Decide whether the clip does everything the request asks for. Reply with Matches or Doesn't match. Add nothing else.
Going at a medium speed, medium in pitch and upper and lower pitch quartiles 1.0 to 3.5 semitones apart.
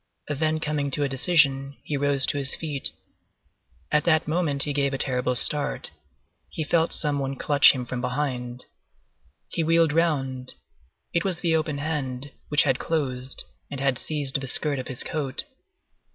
Matches